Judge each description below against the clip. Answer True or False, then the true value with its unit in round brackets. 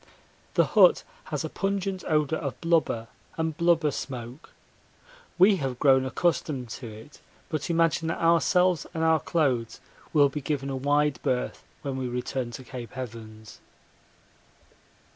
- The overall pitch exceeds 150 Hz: False (145 Hz)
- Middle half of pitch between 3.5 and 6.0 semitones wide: True (4.5 semitones)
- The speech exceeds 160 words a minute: False (145 wpm)